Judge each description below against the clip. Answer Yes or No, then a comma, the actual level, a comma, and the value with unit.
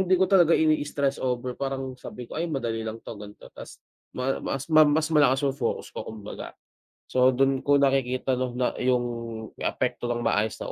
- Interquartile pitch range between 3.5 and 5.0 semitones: No, average, 2.7 semitones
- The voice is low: Yes, low, 130 Hz